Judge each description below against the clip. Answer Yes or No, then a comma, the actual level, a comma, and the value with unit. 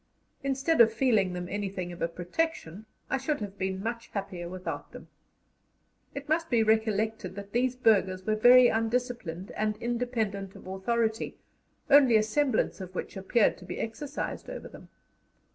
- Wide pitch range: No, average, 4.4 semitones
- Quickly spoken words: No, average, 160 wpm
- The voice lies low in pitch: No, high, 220 Hz